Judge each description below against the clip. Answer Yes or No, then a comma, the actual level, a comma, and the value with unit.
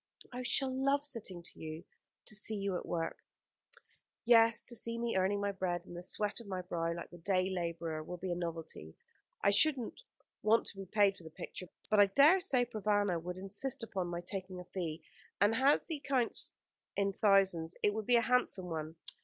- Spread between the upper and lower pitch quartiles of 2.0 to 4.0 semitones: No, average, 4.7 semitones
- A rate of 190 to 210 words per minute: Yes, fast, 205 wpm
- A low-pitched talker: No, high, 195 Hz